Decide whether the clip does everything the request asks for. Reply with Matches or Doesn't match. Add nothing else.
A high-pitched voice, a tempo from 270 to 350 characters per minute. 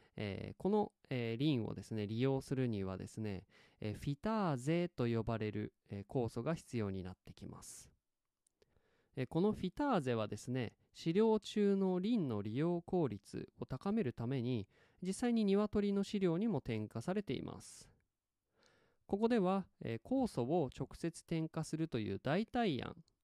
Doesn't match